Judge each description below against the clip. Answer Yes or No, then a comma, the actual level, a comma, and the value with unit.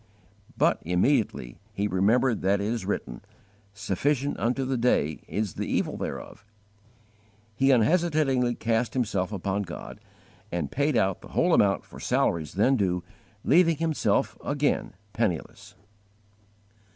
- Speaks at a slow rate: Yes, slow, 125 wpm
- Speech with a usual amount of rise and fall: No, wide, 5.9 semitones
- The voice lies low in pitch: Yes, low, 115 Hz